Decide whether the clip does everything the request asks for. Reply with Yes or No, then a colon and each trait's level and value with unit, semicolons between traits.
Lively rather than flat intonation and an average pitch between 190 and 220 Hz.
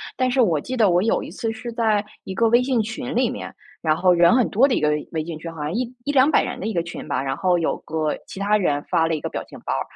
Yes: wide, 6.5 semitones; high, 200 Hz